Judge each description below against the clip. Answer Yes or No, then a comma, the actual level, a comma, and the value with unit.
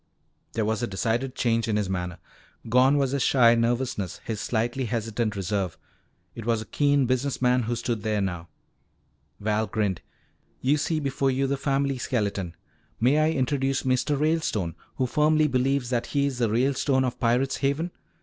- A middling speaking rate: Yes, average, 170 wpm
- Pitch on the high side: No, low, 125 Hz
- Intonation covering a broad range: No, average, 3.8 semitones